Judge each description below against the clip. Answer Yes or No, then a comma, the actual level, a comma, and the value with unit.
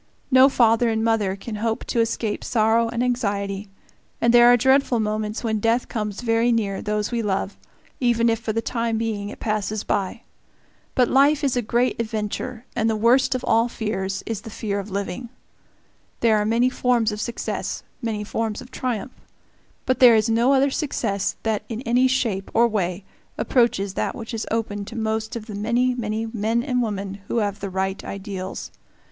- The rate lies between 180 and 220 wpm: Yes, average, 190 wpm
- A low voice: No, high, 225 Hz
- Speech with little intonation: Yes, narrow, 2.3 semitones